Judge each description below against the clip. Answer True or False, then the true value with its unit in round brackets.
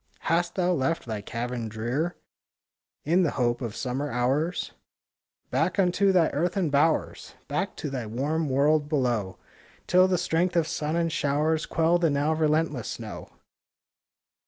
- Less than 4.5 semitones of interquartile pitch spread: False (4.8 semitones)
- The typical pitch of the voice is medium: True (150 Hz)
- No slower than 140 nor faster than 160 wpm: True (145 wpm)